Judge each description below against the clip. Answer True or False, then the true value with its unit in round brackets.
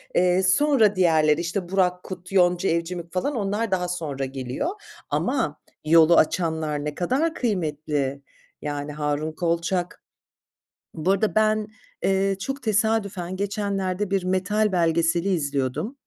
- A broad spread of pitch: False (4.0 semitones)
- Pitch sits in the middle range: True (180 Hz)